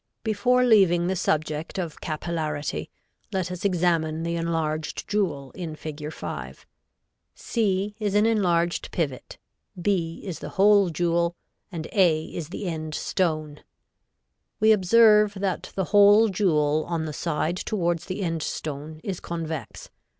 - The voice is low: No, medium, 170 Hz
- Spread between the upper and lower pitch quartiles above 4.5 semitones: No, average, 3.9 semitones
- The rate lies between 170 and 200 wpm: No, slow, 135 wpm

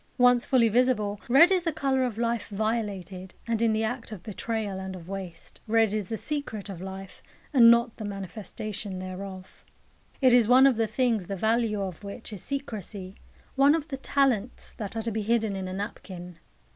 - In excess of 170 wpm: Yes, average, 195 wpm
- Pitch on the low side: No, high, 220 Hz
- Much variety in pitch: No, average, 3.8 semitones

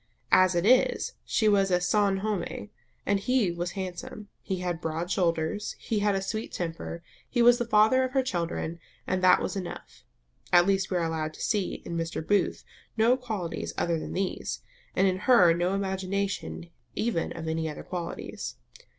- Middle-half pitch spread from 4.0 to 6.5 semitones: No, average, 3.4 semitones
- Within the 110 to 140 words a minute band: No, average, 175 wpm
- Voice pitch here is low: No, high, 190 Hz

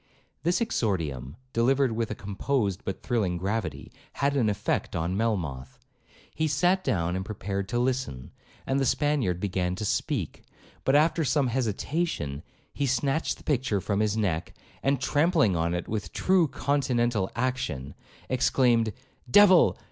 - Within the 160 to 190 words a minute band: No, average, 145 wpm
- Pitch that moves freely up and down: Yes, wide, 6.7 semitones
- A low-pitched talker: Yes, low, 115 Hz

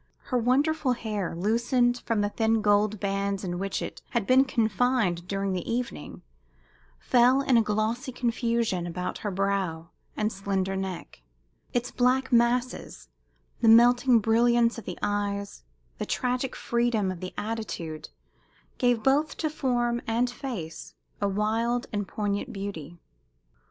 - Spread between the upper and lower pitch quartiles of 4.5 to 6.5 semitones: No, average, 3.7 semitones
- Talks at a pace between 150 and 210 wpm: No, average, 140 wpm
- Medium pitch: No, high, 225 Hz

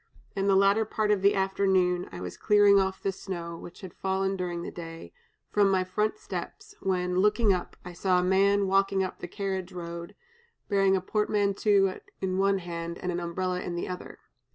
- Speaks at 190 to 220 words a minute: Yes, average, 195 wpm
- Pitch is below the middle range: No, high, 190 Hz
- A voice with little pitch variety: Yes, narrow, 1.8 semitones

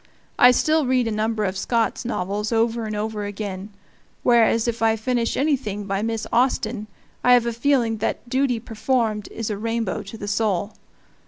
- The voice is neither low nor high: No, high, 225 Hz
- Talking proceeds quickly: No, average, 175 wpm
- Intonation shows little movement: Yes, narrow, 2.3 semitones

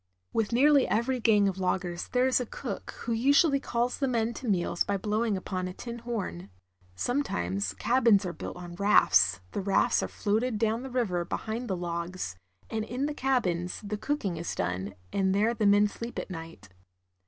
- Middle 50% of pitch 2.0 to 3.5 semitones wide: No, average, 5.2 semitones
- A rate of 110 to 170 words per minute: No, average, 190 wpm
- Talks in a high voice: Yes, high, 210 Hz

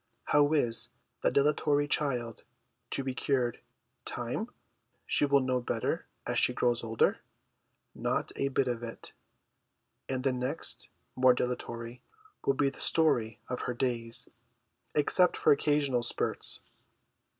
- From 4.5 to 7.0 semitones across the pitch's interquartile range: No, average, 3.0 semitones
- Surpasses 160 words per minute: No, average, 140 wpm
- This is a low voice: Yes, low, 130 Hz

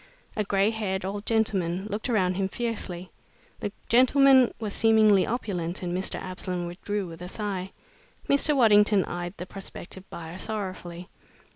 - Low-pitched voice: No, high, 195 Hz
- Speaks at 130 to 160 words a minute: Yes, average, 145 wpm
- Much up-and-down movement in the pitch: No, average, 3.3 semitones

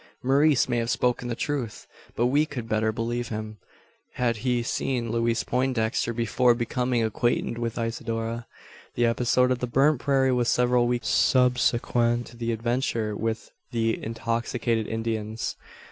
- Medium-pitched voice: No, low, 120 Hz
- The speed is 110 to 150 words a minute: Yes, average, 145 wpm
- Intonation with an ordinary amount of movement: No, narrow, 1.5 semitones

